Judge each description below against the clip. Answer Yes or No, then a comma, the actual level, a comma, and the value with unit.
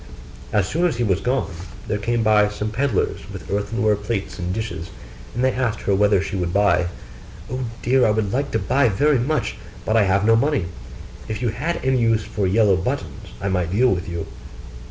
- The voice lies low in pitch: Yes, low, 105 Hz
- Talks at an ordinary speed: No, fast, 210 wpm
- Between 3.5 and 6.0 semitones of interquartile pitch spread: Yes, average, 3.9 semitones